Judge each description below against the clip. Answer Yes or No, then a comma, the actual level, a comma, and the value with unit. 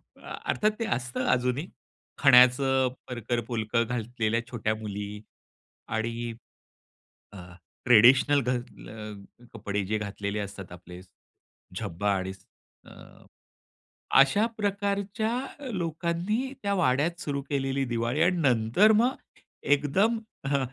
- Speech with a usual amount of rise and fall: No, wide, 7.4 semitones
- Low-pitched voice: Yes, low, 125 Hz